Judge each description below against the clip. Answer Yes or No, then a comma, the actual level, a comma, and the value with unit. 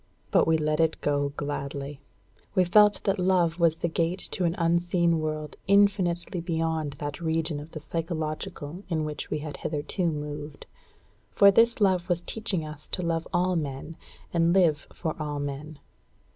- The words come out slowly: No, average, 165 wpm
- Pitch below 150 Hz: No, medium, 165 Hz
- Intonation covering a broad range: No, average, 2.7 semitones